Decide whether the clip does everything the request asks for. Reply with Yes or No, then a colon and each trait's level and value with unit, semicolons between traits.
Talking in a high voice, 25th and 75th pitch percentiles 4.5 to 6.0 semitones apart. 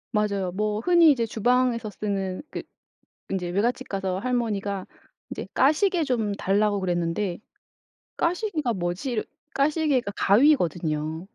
Yes: high, 210 Hz; average, 5.2 semitones